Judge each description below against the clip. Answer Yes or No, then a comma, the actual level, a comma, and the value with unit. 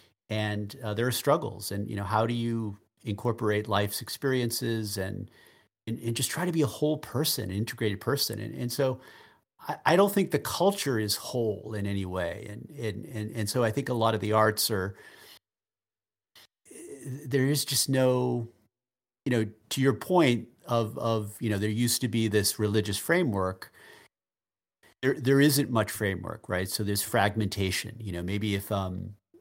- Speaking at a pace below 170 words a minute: No, average, 180 wpm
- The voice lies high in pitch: No, low, 110 Hz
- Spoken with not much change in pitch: No, average, 3.3 semitones